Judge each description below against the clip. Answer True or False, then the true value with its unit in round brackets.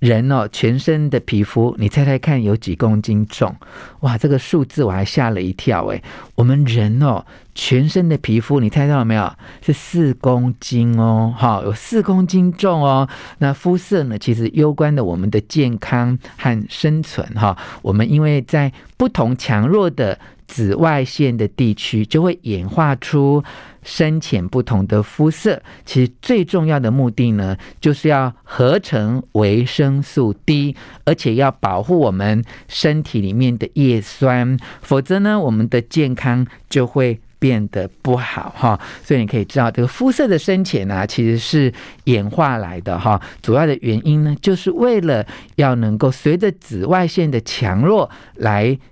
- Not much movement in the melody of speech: False (5.2 semitones)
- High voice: False (130 Hz)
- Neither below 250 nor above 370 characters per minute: False (240 characters per minute)